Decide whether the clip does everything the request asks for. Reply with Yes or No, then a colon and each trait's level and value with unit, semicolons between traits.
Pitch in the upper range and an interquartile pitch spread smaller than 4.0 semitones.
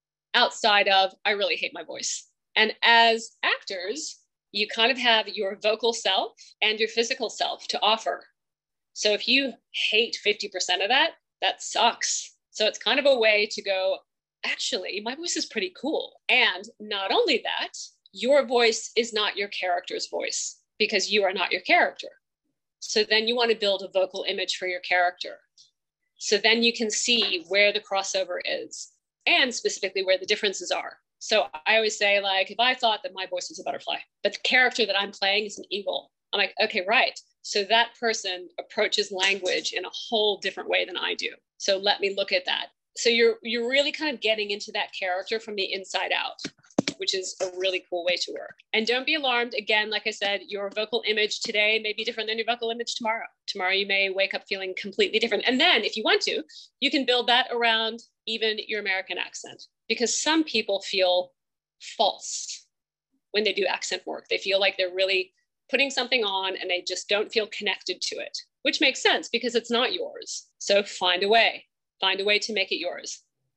Yes: high, 215 Hz; average, 3.5 semitones